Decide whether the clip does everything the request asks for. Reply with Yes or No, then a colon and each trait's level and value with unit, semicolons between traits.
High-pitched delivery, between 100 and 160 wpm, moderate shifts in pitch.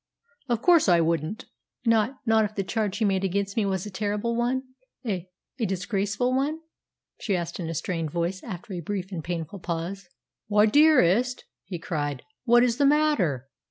No: high, 200 Hz; average, 180 wpm; average, 4.8 semitones